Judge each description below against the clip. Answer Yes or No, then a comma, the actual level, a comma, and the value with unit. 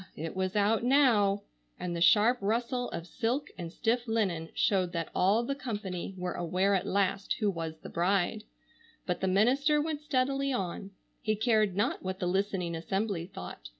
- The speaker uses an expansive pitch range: No, average, 4.6 semitones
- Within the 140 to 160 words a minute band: No, average, 175 wpm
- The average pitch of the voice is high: Yes, high, 200 Hz